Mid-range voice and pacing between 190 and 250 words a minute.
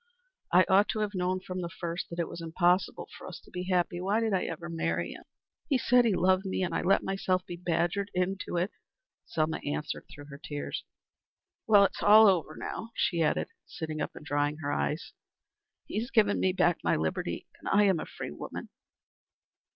Yes: medium, 180 Hz; average, 200 wpm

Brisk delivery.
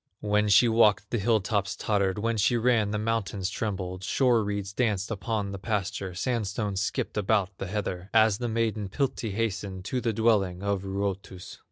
No: average, 175 wpm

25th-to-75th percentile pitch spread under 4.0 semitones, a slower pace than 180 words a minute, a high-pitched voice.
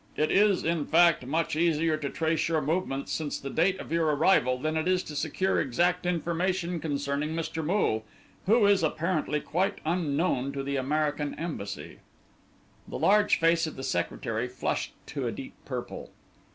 No: average, 3.5 semitones; average, 165 wpm; medium, 160 Hz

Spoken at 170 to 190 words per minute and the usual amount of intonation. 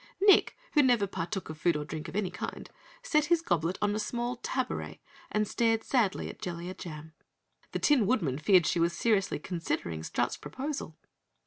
No: average, 180 wpm; wide, 6.5 semitones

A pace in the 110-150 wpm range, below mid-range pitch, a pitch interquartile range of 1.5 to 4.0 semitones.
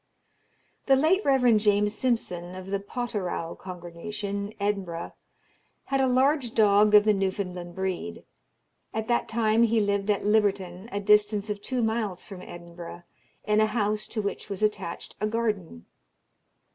No: average, 145 wpm; high, 205 Hz; average, 2.8 semitones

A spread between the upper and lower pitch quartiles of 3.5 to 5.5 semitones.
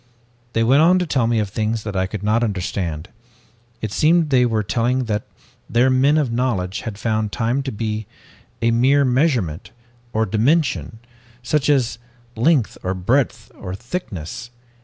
Yes: average, 3.9 semitones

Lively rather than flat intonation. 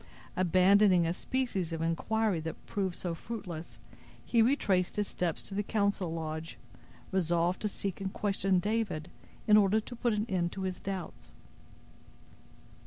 No: average, 3.4 semitones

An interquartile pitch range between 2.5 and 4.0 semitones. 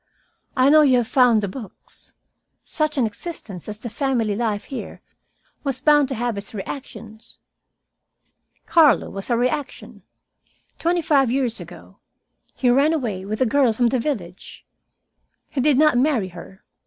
No: average, 4.7 semitones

